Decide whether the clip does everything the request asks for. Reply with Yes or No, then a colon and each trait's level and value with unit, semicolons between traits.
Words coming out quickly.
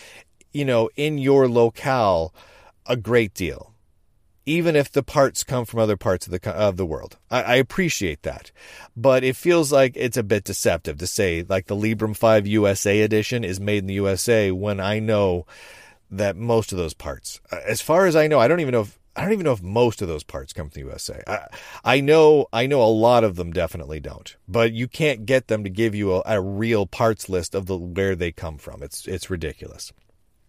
Yes: fast, 215 wpm